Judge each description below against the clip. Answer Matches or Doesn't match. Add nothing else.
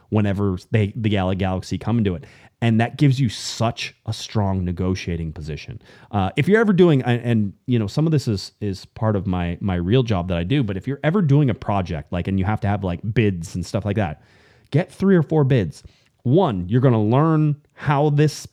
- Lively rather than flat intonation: Matches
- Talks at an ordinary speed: Doesn't match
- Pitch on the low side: Matches